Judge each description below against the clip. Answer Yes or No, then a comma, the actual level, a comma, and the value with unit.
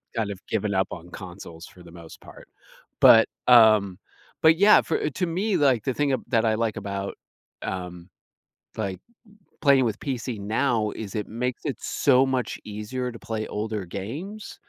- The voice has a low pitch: Yes, low, 110 Hz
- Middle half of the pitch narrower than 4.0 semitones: No, average, 4.8 semitones